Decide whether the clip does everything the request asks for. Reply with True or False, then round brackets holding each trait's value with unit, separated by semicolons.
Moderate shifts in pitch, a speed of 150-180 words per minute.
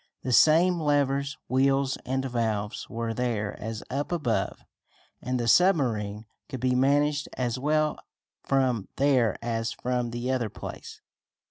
False (3.3 semitones; 135 wpm)